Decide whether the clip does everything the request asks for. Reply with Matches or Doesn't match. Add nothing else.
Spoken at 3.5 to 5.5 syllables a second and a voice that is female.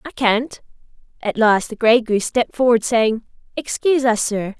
Matches